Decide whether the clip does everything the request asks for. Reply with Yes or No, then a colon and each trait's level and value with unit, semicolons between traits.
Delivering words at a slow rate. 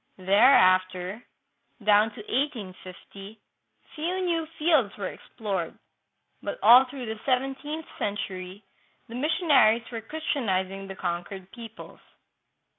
Yes: slow, 110 wpm